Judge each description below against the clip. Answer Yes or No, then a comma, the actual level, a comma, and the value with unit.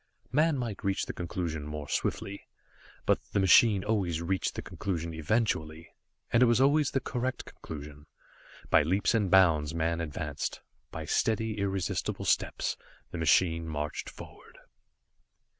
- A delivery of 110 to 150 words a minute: Yes, average, 140 wpm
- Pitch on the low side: Yes, very low, 90 Hz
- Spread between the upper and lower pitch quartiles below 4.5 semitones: No, wide, 5.5 semitones